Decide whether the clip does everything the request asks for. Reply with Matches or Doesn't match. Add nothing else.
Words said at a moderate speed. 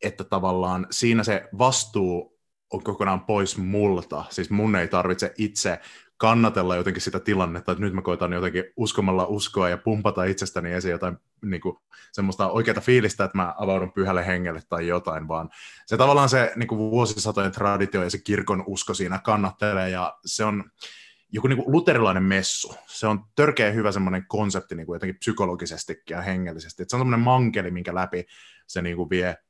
Doesn't match